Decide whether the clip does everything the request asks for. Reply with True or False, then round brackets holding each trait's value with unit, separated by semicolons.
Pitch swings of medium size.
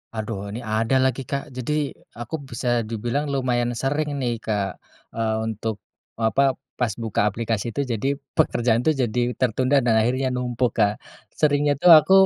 True (3.4 semitones)